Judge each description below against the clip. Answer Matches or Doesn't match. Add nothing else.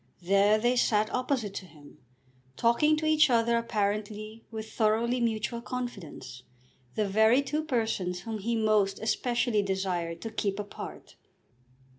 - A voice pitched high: Matches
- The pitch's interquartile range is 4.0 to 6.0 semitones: Doesn't match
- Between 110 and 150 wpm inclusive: Matches